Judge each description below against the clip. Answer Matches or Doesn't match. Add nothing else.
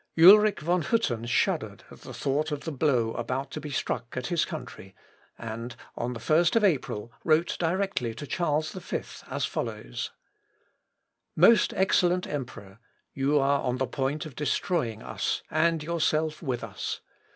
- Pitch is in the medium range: Matches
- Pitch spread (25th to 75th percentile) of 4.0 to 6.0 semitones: Matches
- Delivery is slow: Doesn't match